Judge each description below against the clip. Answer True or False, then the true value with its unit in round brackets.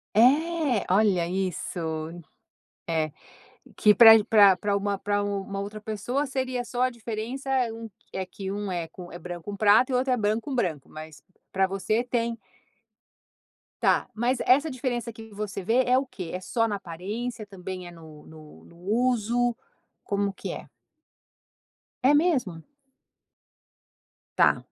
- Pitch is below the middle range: False (210 Hz)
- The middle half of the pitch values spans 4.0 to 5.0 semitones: True (4.4 semitones)